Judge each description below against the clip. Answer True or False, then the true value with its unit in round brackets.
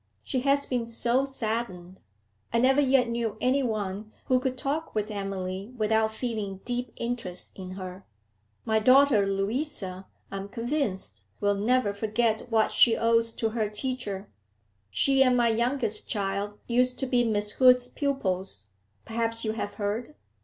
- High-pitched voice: True (225 Hz)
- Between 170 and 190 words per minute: False (155 wpm)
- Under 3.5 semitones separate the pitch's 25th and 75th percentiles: False (3.8 semitones)